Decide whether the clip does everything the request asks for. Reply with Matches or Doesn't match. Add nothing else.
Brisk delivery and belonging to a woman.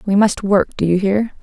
Matches